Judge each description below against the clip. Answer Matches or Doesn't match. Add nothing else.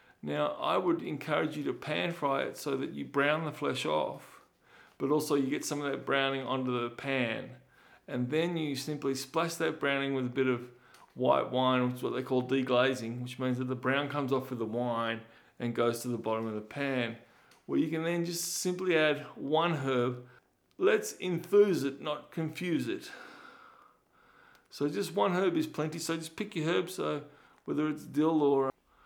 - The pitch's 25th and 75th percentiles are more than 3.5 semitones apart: Matches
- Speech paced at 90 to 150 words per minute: Doesn't match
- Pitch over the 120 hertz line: Matches